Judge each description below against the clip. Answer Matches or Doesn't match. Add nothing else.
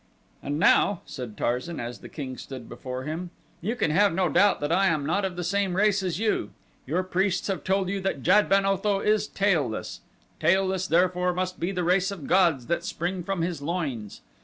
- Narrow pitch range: Doesn't match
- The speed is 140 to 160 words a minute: Doesn't match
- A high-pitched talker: Doesn't match